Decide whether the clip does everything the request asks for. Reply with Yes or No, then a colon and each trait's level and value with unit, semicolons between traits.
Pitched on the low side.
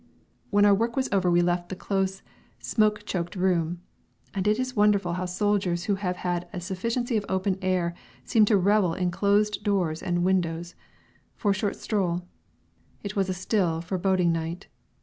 No: high, 190 Hz